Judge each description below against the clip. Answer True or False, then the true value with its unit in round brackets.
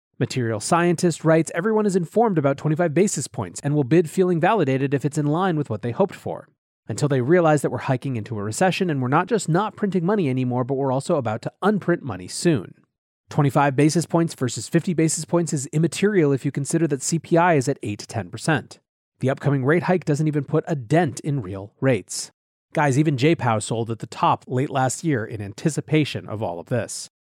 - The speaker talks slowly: False (205 wpm)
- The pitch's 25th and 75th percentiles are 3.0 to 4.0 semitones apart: False (4.6 semitones)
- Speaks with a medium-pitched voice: True (150 Hz)